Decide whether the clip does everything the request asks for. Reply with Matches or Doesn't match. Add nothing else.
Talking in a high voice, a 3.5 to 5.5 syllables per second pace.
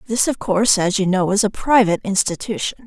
Doesn't match